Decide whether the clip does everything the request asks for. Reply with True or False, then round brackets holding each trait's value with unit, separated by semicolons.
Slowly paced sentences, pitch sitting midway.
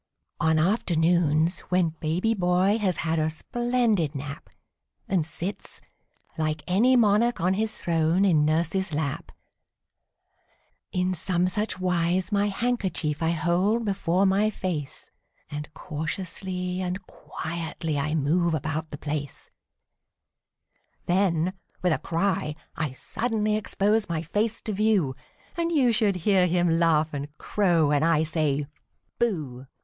True (130 wpm; 175 Hz)